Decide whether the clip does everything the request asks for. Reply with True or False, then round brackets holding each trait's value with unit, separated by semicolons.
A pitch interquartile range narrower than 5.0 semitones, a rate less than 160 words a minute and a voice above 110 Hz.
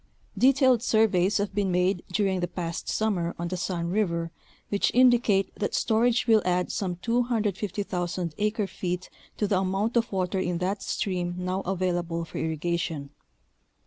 True (3.3 semitones; 150 wpm; 190 Hz)